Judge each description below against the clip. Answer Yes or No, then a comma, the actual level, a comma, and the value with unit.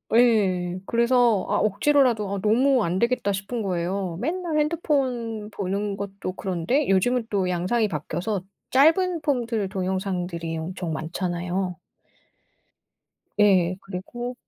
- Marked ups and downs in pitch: No, average, 5.0 semitones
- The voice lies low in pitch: No, high, 200 Hz